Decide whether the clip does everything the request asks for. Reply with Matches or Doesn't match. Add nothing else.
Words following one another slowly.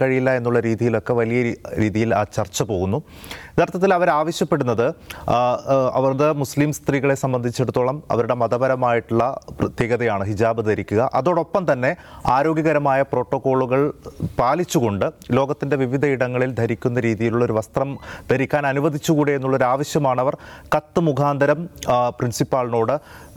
Matches